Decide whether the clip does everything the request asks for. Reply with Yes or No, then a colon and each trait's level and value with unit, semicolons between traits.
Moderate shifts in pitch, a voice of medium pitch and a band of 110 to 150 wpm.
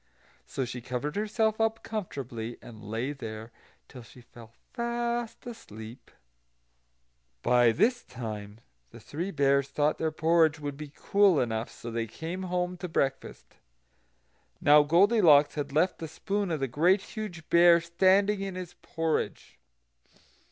No: wide, 7.3 semitones; medium, 155 Hz; average, 140 wpm